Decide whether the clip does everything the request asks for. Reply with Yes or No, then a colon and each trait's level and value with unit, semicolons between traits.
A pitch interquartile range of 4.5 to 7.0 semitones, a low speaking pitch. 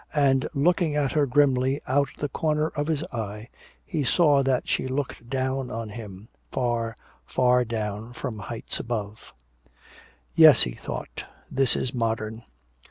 No: average, 3.9 semitones; low, 130 Hz